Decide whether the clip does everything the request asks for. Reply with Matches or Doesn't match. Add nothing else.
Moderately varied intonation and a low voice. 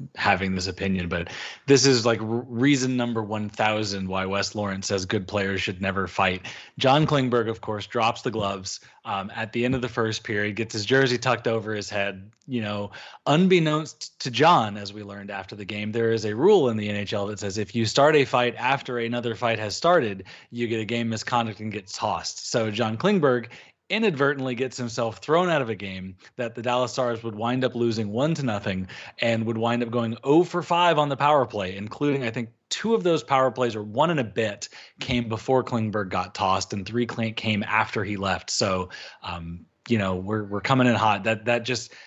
Matches